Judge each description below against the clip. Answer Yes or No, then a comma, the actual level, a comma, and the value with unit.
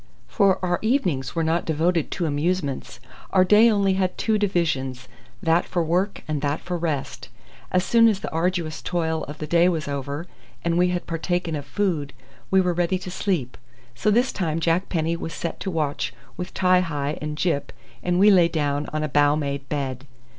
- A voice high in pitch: No, medium, 170 Hz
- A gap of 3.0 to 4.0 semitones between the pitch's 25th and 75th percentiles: Yes, average, 3.6 semitones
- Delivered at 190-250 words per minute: Yes, average, 195 wpm